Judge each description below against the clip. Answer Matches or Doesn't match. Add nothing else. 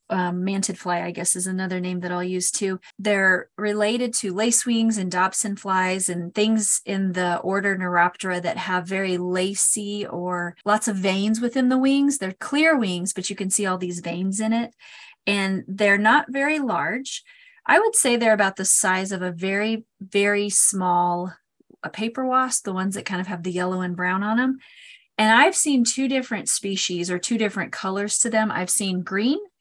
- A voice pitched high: Matches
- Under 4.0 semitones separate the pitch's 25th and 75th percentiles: Matches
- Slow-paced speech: Doesn't match